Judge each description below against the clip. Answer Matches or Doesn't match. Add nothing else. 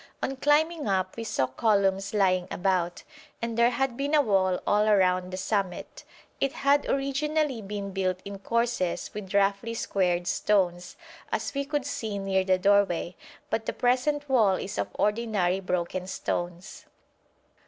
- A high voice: Matches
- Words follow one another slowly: Doesn't match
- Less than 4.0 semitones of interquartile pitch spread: Doesn't match